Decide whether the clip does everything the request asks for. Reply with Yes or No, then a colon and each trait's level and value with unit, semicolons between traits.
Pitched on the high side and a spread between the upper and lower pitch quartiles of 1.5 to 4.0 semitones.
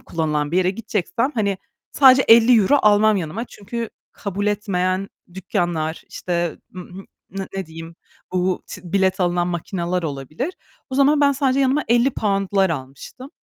No: high, 195 Hz; average, 4.8 semitones